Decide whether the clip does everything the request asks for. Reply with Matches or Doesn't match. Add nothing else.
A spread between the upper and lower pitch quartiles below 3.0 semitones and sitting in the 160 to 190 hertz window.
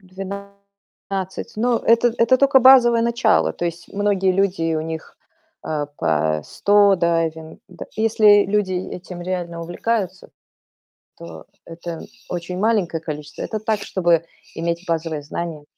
Doesn't match